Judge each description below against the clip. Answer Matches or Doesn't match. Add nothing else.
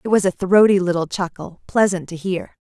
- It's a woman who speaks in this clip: Matches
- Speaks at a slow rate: Doesn't match